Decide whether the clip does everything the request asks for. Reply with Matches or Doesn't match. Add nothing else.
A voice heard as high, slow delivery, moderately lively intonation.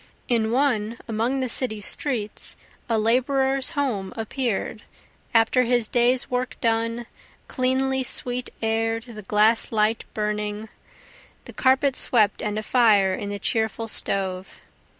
Matches